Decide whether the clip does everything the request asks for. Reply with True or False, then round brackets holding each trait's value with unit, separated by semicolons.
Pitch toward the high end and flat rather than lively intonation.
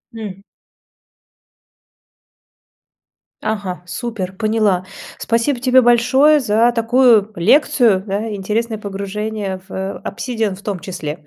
False (215 Hz; 3.5 semitones)